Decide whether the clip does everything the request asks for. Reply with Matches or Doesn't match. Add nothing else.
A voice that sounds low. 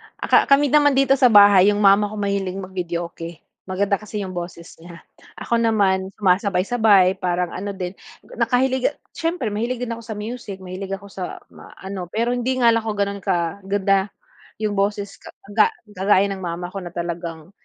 Doesn't match